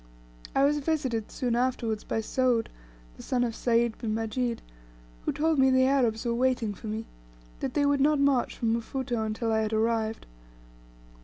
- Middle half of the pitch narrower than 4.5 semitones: Yes, average, 2.9 semitones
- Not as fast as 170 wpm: No, average, 175 wpm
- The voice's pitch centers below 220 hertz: No, high, 235 Hz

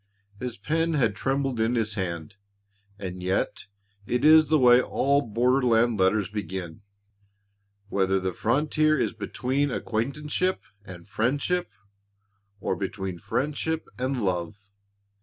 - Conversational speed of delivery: No, slow, 120 wpm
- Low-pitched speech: Yes, low, 120 Hz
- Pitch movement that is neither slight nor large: No, wide, 6.2 semitones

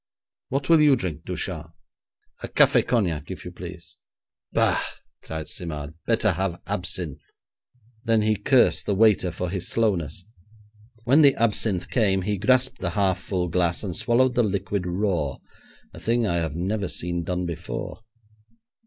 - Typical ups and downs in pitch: Yes, average, 4.5 semitones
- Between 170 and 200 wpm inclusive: No, average, 155 wpm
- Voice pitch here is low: Yes, very low, 95 Hz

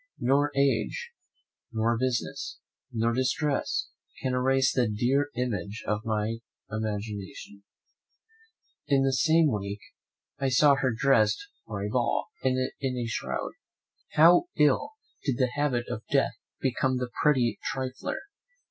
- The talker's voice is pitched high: No, low, 125 Hz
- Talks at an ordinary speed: No, slow, 130 wpm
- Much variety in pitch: No, average, 3.5 semitones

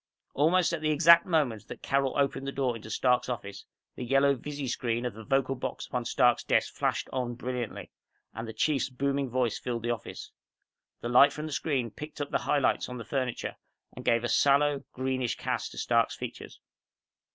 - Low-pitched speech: Yes, low, 130 Hz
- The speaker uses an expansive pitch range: No, average, 2.9 semitones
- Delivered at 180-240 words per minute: Yes, average, 195 wpm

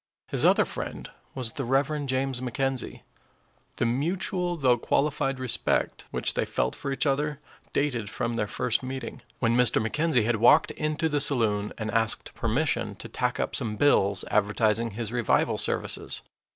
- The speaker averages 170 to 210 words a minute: No, average, 160 wpm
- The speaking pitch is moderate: No, low, 125 Hz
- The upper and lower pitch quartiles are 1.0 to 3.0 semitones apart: No, average, 3.9 semitones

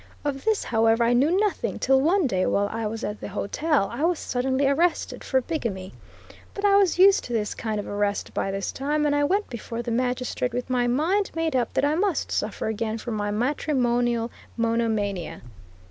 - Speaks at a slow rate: No, average, 200 wpm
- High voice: Yes, high, 245 Hz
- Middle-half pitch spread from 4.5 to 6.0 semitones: Yes, average, 5.2 semitones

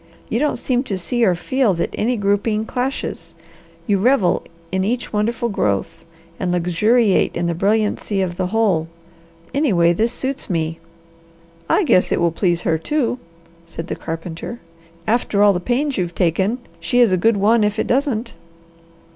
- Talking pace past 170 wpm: No, average, 165 wpm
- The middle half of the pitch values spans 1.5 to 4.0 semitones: No, average, 5.2 semitones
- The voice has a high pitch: Yes, high, 205 Hz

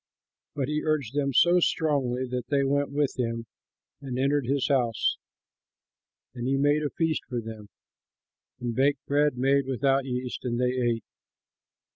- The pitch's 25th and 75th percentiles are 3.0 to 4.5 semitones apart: No, narrow, 2.5 semitones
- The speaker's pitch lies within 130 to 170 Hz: Yes, low, 135 Hz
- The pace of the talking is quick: No, average, 155 wpm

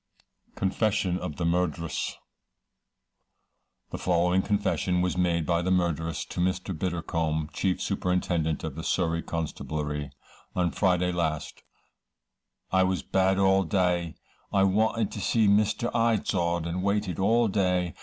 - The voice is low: Yes, very low, 90 Hz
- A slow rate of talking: Yes, slow, 130 wpm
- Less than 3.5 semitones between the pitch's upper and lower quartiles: Yes, narrow, 2.4 semitones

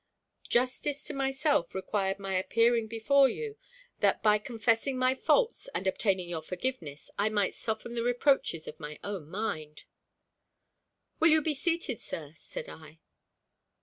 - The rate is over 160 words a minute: No, average, 145 wpm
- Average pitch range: No, wide, 6.1 semitones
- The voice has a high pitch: Yes, high, 220 Hz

